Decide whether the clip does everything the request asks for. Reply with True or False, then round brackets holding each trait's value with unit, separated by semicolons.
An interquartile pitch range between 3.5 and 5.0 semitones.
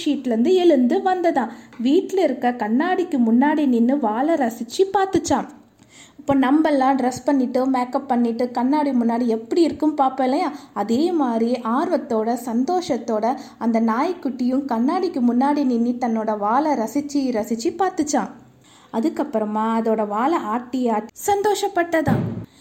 True (4.2 semitones)